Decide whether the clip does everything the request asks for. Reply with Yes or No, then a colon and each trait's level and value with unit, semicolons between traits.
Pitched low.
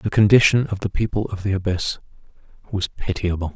Yes: low, 100 Hz